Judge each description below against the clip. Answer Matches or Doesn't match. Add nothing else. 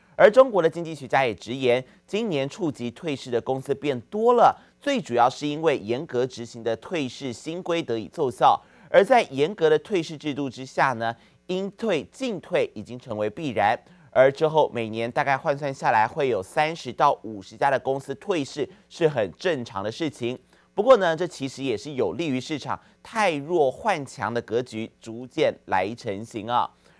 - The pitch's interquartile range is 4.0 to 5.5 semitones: Matches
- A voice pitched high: Doesn't match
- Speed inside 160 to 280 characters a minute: Matches